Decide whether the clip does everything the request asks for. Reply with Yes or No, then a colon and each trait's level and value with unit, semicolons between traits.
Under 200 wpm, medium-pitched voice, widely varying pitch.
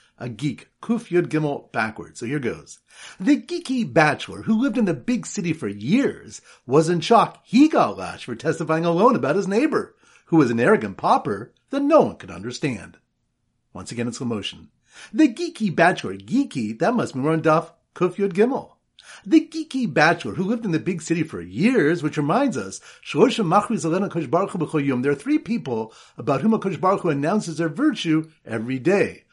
Yes: average, 175 wpm; medium, 175 Hz; wide, 7.5 semitones